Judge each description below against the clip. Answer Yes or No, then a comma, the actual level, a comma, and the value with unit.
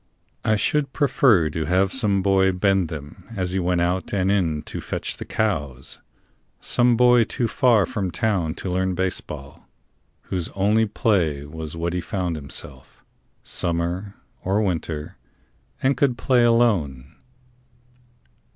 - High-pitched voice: No, very low, 95 Hz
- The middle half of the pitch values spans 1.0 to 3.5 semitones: No, average, 4.7 semitones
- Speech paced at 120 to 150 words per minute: Yes, average, 140 wpm